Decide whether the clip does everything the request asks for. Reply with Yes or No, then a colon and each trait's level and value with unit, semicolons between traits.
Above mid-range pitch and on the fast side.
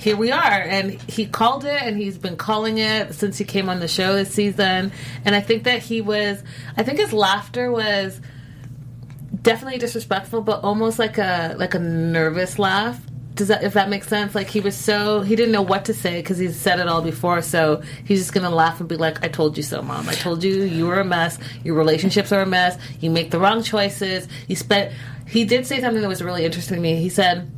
Yes: high, 195 Hz; fast, 235 wpm